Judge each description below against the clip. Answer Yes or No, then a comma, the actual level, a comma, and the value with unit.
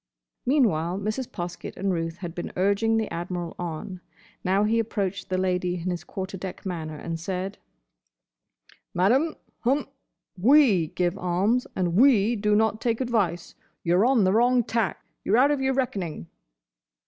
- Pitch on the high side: Yes, high, 195 Hz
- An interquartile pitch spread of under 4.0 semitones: No, average, 4.5 semitones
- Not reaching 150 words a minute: No, average, 155 wpm